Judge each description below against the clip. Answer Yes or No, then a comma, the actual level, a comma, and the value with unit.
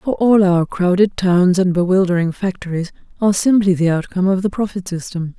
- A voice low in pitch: No, medium, 185 Hz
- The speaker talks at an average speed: Yes, average, 180 wpm